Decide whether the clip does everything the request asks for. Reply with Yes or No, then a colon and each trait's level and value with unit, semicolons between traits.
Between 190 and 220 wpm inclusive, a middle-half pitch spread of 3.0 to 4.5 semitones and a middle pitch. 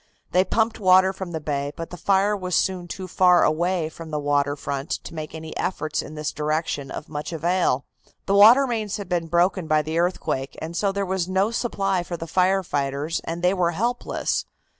Yes: fast, 205 wpm; average, 3.5 semitones; medium, 175 Hz